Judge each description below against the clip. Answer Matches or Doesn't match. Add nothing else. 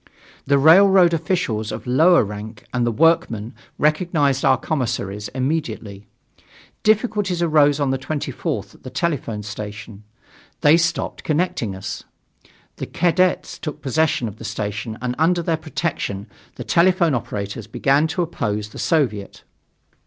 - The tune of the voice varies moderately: Doesn't match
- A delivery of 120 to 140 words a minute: Matches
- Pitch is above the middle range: Doesn't match